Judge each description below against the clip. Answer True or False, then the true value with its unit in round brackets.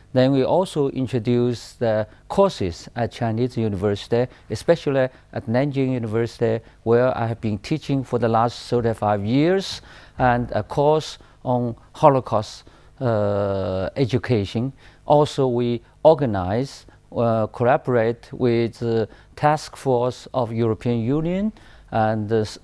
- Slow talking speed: True (120 wpm)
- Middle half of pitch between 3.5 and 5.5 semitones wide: False (2.9 semitones)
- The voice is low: True (120 Hz)